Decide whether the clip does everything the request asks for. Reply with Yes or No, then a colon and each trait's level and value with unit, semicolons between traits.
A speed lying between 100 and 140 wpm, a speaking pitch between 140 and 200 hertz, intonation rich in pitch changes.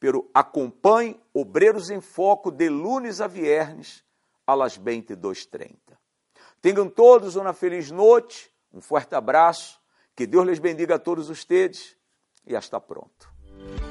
Yes: average, 130 wpm; high, 190 Hz; wide, 8.6 semitones